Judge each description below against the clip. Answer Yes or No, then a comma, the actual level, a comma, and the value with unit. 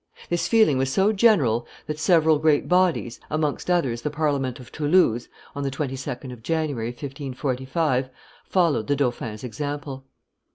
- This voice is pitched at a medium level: Yes, medium, 145 Hz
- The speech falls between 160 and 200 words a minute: No, average, 140 wpm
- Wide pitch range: No, average, 3.6 semitones